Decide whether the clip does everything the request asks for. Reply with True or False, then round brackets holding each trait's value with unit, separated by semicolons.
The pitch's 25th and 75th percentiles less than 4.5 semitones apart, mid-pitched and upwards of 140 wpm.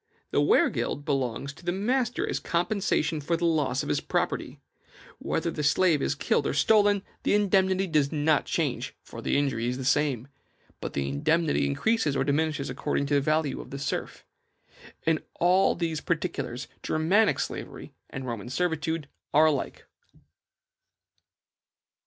True (4.0 semitones; 155 Hz; 155 wpm)